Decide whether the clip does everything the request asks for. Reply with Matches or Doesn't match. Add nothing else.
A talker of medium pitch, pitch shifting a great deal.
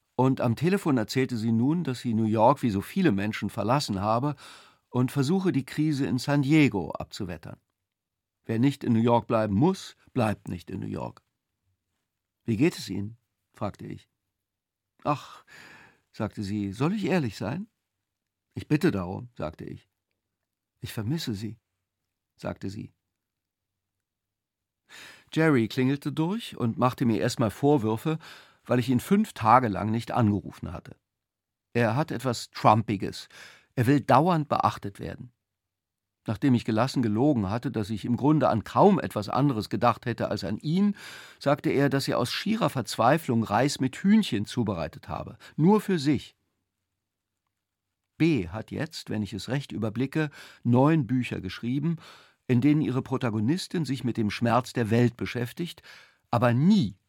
Doesn't match